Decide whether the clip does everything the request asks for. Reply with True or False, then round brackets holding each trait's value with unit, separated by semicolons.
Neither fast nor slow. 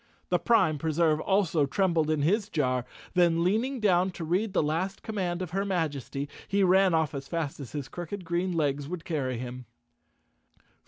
True (175 wpm)